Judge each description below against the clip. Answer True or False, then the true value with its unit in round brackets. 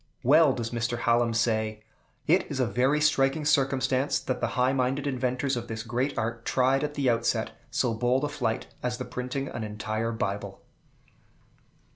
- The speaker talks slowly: False (170 wpm)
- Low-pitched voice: True (125 Hz)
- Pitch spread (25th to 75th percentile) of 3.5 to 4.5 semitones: False (2.7 semitones)